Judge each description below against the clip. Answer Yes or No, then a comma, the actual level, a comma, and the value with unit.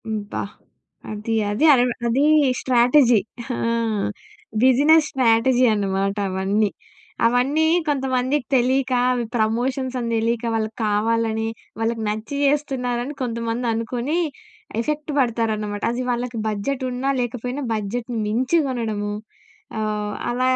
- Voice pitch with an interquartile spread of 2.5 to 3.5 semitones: Yes, average, 2.9 semitones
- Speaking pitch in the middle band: No, high, 240 Hz